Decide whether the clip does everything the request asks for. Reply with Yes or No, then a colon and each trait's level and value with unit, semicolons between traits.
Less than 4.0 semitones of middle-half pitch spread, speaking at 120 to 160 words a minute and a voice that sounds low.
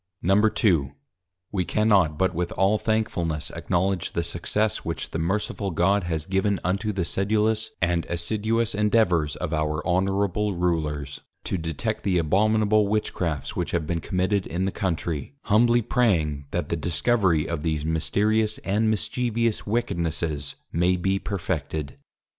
No: average, 4.4 semitones; average, 140 wpm; very low, 95 Hz